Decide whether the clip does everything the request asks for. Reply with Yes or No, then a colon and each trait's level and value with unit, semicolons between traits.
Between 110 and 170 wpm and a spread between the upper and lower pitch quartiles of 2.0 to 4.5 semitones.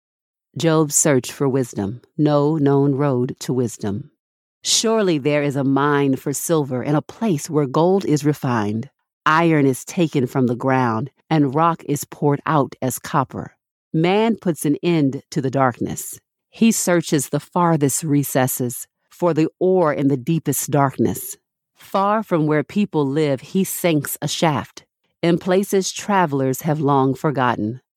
Yes: average, 150 wpm; average, 3.7 semitones